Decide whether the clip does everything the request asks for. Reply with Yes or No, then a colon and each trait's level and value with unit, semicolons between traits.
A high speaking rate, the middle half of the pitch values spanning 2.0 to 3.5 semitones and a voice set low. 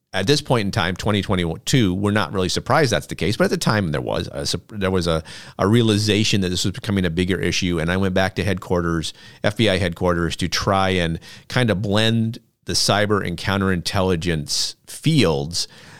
No: average, 190 wpm; average, 2.9 semitones; very low, 95 Hz